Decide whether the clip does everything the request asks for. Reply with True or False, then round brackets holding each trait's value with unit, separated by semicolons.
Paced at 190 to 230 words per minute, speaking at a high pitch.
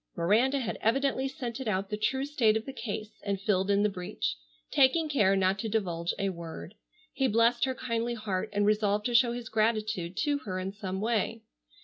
True (200 wpm; 215 Hz)